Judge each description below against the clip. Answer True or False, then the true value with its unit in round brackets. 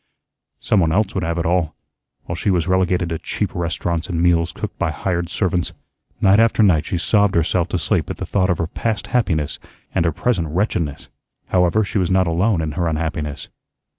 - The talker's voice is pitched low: True (85 Hz)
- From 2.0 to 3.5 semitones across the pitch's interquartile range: True (2.6 semitones)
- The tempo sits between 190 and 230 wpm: True (200 wpm)